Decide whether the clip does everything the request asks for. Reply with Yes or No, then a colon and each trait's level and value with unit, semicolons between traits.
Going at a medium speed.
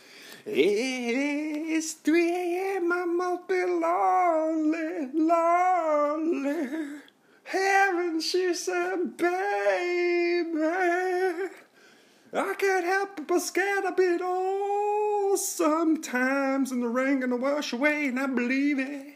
No: slow, 110 wpm